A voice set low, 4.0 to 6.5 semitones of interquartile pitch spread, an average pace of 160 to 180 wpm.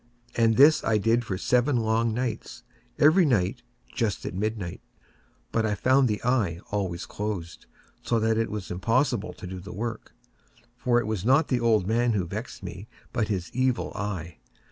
No: low, 110 Hz; average, 3.6 semitones; average, 165 wpm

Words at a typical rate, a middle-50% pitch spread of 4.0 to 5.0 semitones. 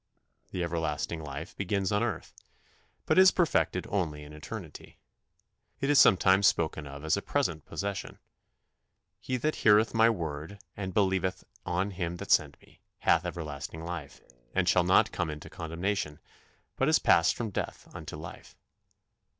Yes: average, 150 wpm; average, 4.4 semitones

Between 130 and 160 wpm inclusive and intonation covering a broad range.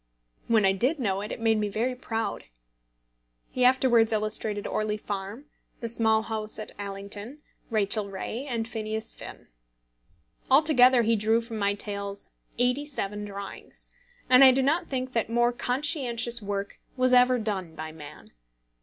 No: average, 155 wpm; average, 3.4 semitones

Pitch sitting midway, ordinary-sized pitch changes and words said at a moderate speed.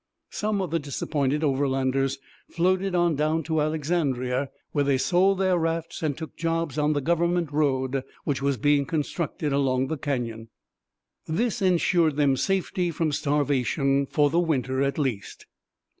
Yes: medium, 150 Hz; average, 3.4 semitones; average, 150 wpm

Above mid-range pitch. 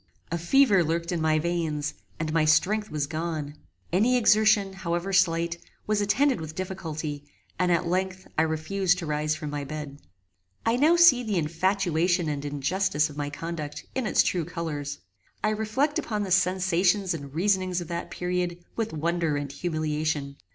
No: medium, 170 Hz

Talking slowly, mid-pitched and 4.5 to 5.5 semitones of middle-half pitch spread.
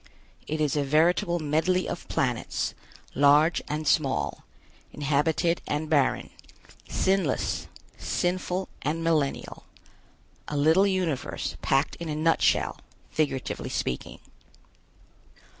No: slow, 100 wpm; medium, 155 Hz; average, 2.9 semitones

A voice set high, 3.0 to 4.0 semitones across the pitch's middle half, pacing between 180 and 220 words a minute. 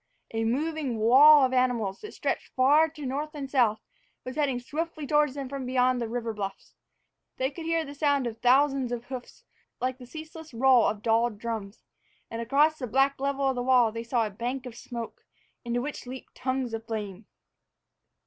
Yes: very high, 255 Hz; average, 3.4 semitones; average, 190 wpm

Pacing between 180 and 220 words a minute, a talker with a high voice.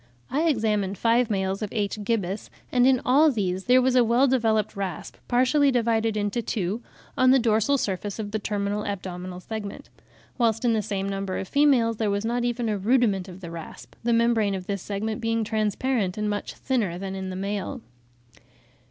Yes: average, 190 wpm; high, 215 Hz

